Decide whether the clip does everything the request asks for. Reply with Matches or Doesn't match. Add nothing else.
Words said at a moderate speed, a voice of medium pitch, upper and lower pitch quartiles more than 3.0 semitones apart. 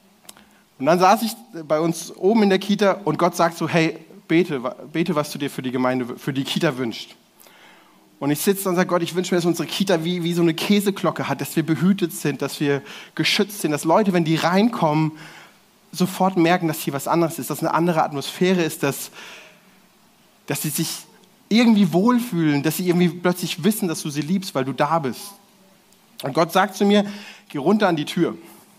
Doesn't match